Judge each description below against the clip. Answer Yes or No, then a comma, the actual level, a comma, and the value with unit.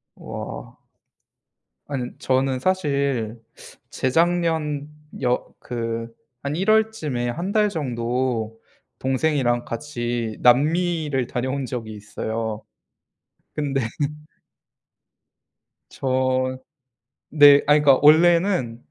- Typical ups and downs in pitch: Yes, average, 4.1 semitones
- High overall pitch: No, low, 130 Hz